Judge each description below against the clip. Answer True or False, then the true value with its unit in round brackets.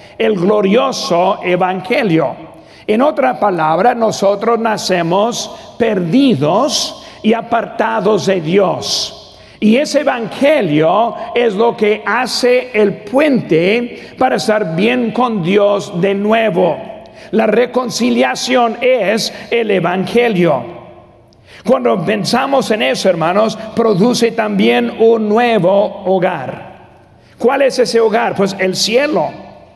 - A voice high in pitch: True (220 Hz)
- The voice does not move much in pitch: False (3.5 semitones)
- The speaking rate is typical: False (105 wpm)